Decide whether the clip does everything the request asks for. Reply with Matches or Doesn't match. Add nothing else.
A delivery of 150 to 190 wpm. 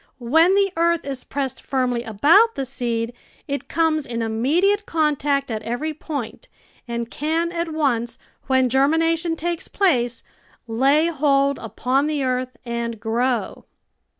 Doesn't match